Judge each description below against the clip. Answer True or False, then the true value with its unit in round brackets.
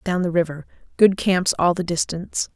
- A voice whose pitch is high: False (175 Hz)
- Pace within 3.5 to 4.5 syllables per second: False (5.2 syllables/s)